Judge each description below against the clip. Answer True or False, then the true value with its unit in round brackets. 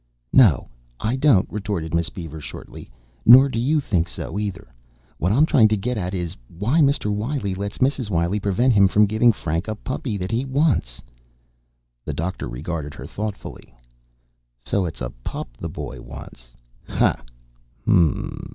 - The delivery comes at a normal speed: True (160 wpm)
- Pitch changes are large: True (6.2 semitones)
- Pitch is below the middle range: True (100 Hz)